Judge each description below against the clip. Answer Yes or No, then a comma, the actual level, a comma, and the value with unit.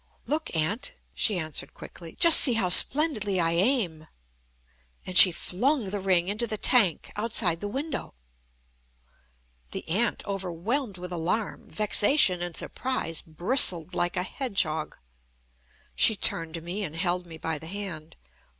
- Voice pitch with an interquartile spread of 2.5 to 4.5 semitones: No, average, 5.0 semitones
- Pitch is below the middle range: No, medium, 185 Hz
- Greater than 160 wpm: No, average, 140 wpm